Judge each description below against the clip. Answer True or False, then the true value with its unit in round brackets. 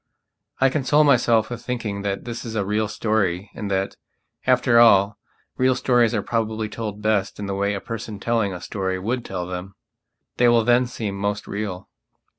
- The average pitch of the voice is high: False (110 Hz)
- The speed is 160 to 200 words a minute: True (185 wpm)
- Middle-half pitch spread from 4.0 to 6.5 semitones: False (3.0 semitones)